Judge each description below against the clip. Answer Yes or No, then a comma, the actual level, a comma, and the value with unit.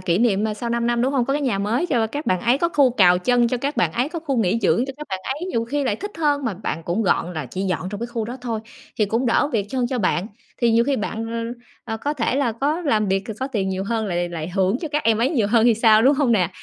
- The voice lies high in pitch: Yes, high, 230 Hz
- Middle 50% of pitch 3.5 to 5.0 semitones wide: Yes, average, 4.6 semitones